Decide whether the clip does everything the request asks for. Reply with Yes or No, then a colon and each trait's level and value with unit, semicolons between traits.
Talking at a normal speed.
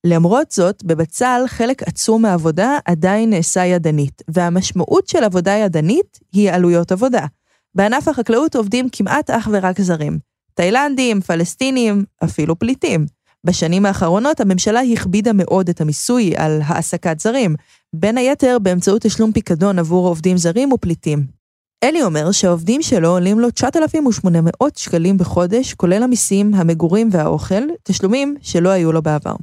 Yes: average, 130 wpm